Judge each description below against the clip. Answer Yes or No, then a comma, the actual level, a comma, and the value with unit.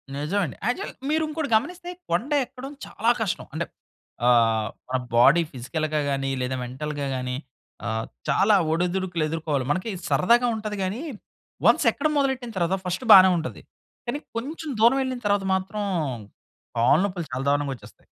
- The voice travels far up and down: Yes, wide, 8.9 semitones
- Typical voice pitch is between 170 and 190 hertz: Yes, medium, 180 Hz